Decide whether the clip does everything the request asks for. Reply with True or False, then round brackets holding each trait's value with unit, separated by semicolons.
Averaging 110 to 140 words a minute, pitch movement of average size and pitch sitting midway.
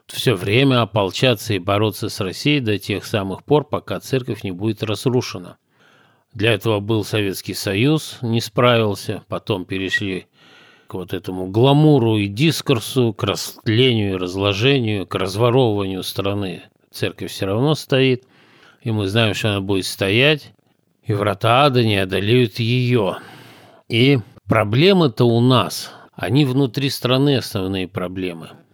False (135 wpm; 4.6 semitones; 110 Hz)